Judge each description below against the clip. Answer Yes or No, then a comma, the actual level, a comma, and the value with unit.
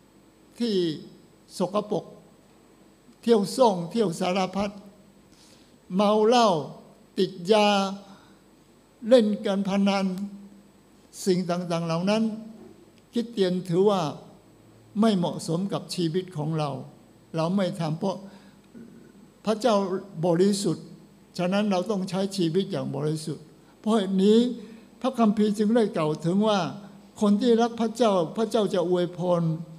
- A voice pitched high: Yes, high, 195 Hz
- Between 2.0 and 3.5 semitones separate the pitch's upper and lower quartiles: Yes, average, 3.2 semitones